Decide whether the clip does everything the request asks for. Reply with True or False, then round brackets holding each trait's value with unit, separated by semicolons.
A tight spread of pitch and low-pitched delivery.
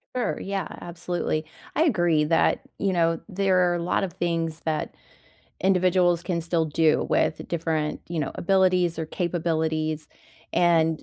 False (2.2 semitones; 170 Hz)